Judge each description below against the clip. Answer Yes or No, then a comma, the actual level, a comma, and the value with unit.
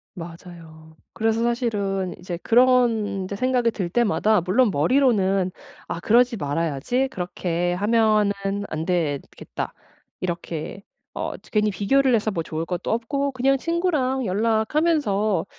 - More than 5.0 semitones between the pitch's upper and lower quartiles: Yes, wide, 5.6 semitones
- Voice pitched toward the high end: Yes, high, 210 Hz